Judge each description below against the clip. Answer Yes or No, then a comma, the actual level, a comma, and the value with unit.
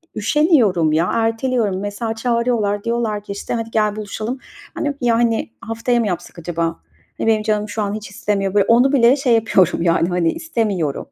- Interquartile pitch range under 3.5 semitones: Yes, average, 2.9 semitones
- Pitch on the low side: No, high, 215 Hz